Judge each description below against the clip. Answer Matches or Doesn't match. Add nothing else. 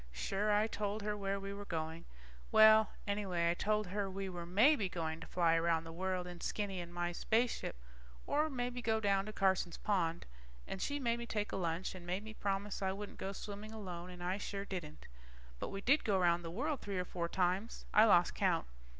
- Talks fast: Matches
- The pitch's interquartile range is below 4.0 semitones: Matches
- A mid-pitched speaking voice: Doesn't match